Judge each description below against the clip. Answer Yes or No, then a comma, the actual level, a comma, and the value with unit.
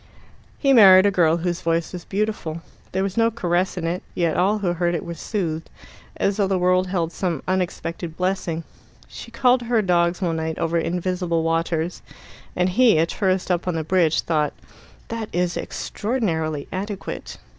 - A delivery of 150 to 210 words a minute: Yes, average, 175 wpm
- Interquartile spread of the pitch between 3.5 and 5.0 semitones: No, average, 2.7 semitones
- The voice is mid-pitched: Yes, medium, 180 Hz